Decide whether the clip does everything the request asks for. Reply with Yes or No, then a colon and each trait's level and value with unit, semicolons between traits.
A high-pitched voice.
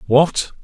No: medium, 145 Hz